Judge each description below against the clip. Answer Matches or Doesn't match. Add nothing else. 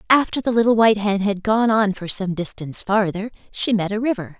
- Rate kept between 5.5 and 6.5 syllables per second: Matches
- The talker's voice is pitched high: Matches